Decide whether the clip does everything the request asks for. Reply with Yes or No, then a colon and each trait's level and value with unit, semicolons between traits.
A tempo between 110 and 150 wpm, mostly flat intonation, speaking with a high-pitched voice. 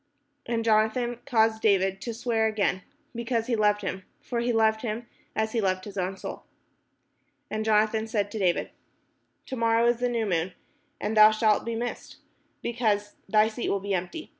No: average, 180 wpm; narrow, 2.1 semitones; high, 220 Hz